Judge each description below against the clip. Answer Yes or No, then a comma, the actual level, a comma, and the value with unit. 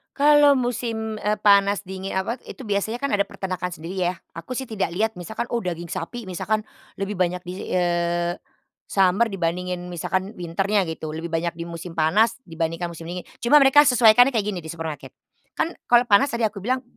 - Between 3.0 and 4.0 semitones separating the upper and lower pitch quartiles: No, average, 4.6 semitones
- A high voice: Yes, high, 195 Hz